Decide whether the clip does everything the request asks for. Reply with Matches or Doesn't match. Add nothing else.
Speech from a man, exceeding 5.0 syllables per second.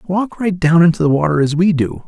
Matches